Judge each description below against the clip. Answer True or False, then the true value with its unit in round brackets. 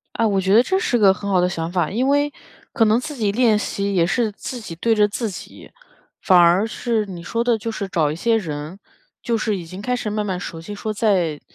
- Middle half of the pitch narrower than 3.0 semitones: False (4.1 semitones)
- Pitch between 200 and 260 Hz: True (210 Hz)